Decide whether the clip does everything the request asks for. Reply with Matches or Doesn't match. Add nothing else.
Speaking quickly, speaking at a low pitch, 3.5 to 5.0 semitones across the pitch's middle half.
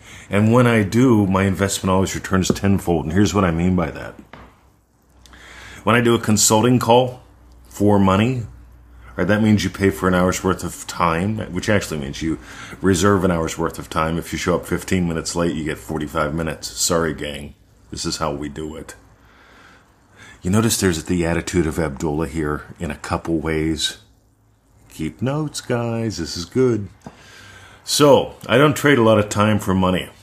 Doesn't match